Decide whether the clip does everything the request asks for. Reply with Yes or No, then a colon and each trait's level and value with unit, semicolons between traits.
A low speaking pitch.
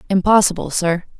No: medium, 185 Hz